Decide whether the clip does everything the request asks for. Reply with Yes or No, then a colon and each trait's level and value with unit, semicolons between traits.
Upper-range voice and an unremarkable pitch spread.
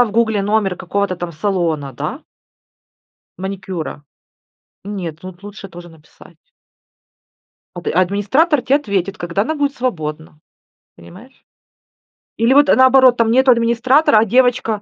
No: high, 205 Hz; wide, 5.8 semitones